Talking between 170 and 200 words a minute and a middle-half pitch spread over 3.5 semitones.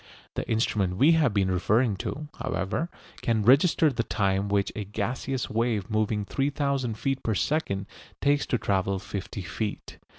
No: average, 155 wpm; wide, 5.4 semitones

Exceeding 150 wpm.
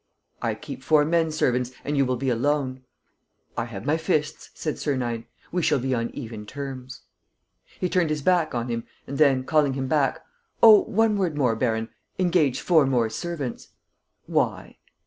Yes: average, 170 wpm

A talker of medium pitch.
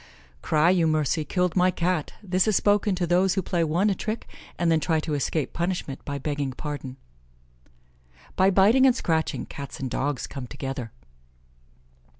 Yes: medium, 165 Hz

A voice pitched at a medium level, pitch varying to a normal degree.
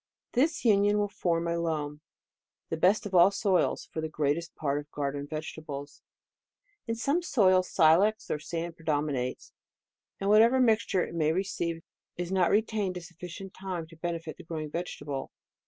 Yes: medium, 170 Hz; average, 4.2 semitones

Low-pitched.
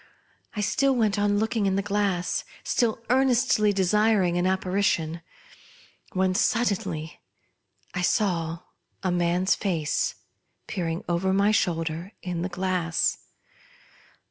No: high, 190 Hz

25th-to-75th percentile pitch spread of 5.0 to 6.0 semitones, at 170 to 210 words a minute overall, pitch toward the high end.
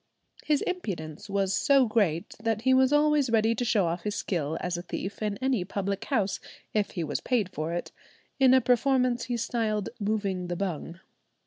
Yes: wide, 5.4 semitones; average, 190 wpm; high, 210 Hz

